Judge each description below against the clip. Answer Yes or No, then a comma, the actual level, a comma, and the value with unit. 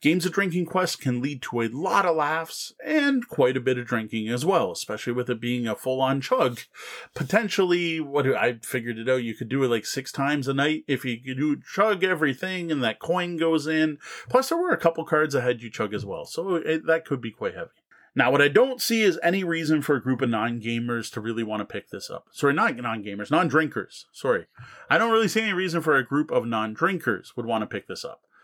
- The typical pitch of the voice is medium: Yes, medium, 145 Hz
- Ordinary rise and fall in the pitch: No, wide, 6.3 semitones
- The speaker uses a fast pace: Yes, fast, 235 wpm